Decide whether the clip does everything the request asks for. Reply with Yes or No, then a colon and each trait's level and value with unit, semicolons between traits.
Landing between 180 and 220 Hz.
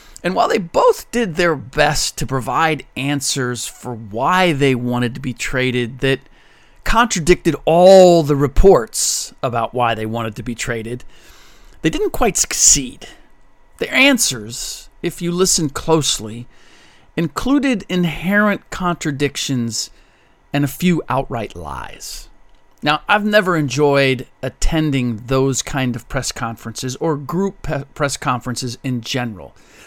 No: medium, 140 Hz